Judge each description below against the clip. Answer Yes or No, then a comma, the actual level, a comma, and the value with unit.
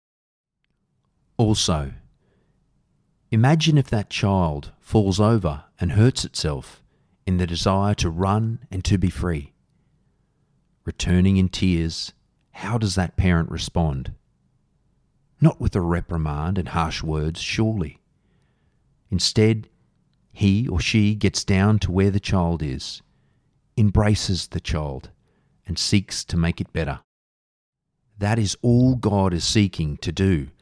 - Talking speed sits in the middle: No, slow, 125 wpm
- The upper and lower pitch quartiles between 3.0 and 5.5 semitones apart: Yes, average, 4.1 semitones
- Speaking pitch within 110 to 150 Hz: No, very low, 95 Hz